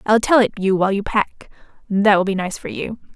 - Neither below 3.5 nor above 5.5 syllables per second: No, 5.7 syllables/s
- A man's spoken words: No, female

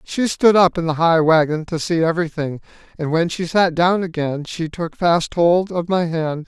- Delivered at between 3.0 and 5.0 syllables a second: Yes, 4.6 syllables/s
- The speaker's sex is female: No, male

